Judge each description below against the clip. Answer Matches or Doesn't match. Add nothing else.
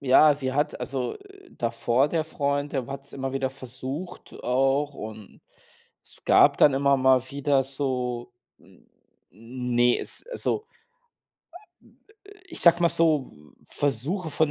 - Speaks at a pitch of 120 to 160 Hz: Matches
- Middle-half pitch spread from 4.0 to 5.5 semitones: Doesn't match